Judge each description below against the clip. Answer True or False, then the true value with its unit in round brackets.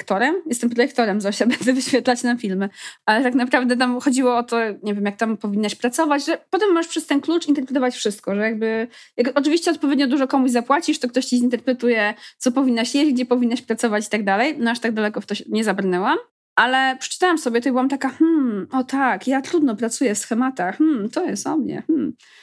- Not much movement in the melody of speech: False (4.0 semitones)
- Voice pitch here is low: False (250 Hz)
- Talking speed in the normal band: False (215 wpm)